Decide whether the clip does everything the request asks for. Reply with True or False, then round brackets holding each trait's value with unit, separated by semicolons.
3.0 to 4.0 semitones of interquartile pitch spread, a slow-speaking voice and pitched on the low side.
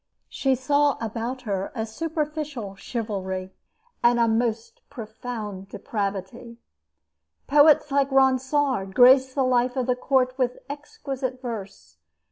False (3.7 semitones; 115 wpm; 245 Hz)